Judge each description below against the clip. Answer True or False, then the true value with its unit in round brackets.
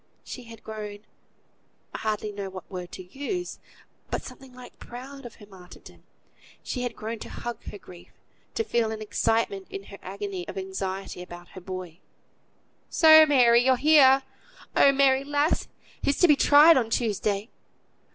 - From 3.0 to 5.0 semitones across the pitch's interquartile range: False (5.5 semitones)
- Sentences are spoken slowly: False (160 wpm)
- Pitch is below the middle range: False (225 Hz)